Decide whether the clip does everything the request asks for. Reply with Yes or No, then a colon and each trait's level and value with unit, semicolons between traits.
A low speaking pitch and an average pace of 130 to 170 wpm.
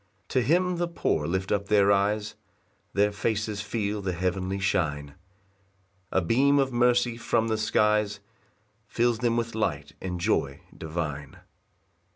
Yes: low, 105 Hz; average, 145 wpm